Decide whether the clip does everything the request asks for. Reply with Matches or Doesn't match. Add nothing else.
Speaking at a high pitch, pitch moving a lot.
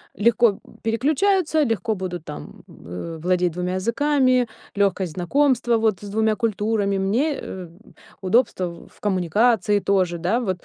Doesn't match